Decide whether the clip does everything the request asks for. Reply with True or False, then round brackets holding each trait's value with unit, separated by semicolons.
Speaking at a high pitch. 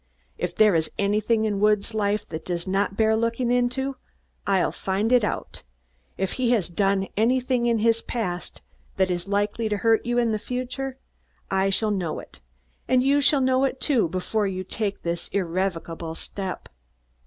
True (210 Hz)